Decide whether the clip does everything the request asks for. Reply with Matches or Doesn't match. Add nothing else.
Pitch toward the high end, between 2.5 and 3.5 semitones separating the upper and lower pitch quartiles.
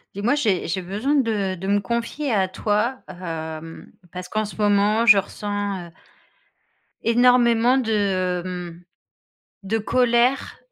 Doesn't match